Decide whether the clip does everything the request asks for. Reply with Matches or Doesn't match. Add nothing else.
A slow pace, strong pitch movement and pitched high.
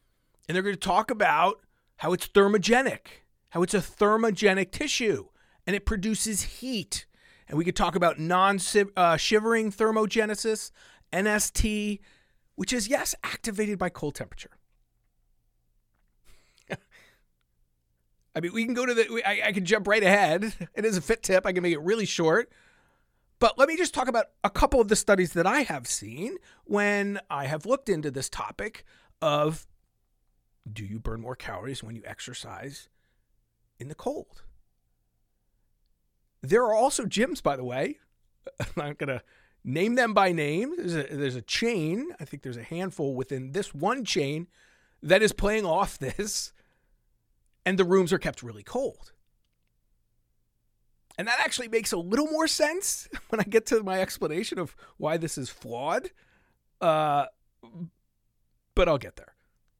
Doesn't match